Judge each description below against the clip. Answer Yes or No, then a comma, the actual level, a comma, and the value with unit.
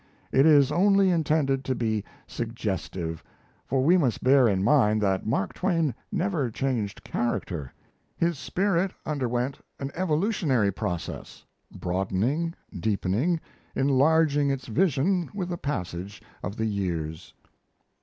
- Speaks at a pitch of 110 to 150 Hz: Yes, low, 135 Hz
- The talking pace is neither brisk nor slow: No, slow, 120 wpm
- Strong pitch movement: Yes, wide, 7.9 semitones